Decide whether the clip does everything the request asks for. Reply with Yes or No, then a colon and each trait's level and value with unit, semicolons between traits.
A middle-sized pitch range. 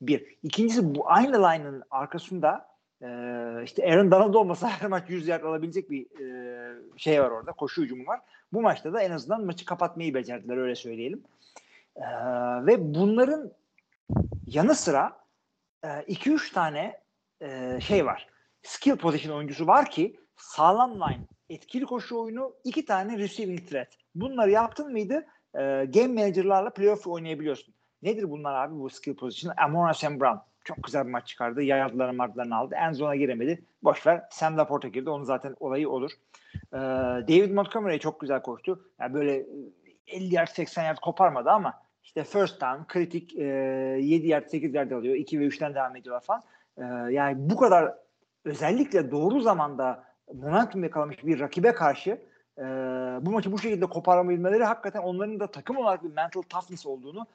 No: wide, 6.7 semitones